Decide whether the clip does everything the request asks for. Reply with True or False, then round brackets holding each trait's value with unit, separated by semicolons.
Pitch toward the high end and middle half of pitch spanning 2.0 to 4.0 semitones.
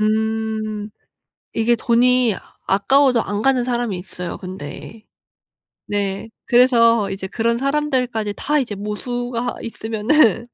True (225 Hz; 2.8 semitones)